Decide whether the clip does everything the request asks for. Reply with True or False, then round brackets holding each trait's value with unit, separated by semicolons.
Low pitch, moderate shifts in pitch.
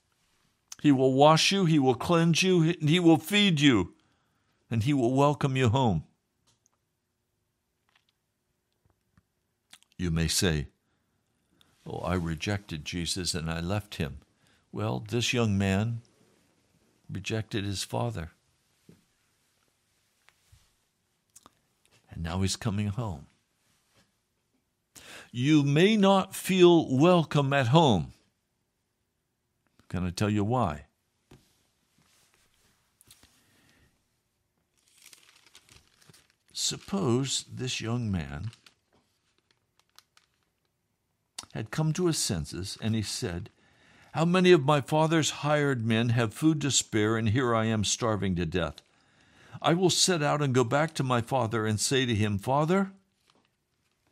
False (120 Hz; 6.9 semitones)